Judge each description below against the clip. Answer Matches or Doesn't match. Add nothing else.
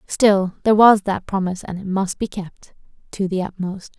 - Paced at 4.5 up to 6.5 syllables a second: Matches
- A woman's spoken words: Matches